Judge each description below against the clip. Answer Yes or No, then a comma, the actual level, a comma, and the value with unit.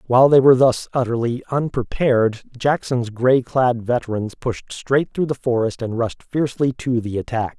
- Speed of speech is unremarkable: Yes, average, 165 wpm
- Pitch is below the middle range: Yes, low, 125 Hz